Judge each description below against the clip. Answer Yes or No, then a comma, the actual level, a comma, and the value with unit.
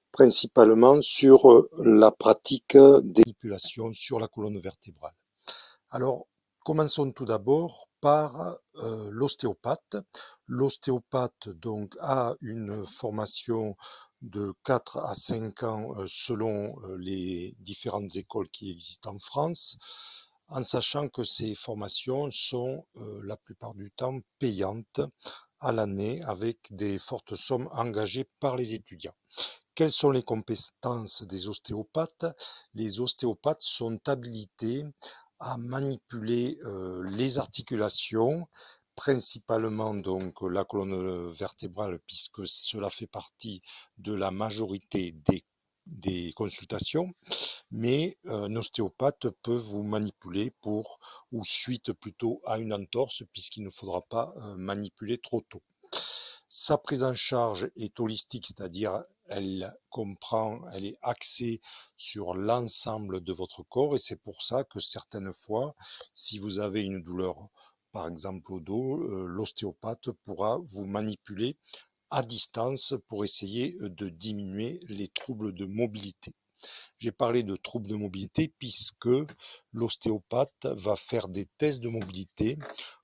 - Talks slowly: Yes, slow, 125 wpm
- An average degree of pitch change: Yes, average, 4.1 semitones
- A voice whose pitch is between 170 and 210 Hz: No, low, 110 Hz